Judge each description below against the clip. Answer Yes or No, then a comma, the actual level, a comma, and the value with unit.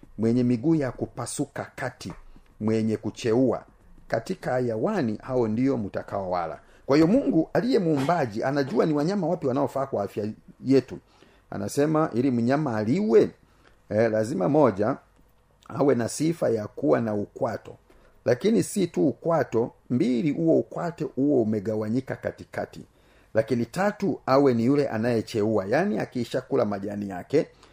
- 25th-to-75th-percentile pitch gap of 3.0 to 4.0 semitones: No, average, 4.6 semitones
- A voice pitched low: Yes, low, 125 Hz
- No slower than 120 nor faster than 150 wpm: Yes, average, 130 wpm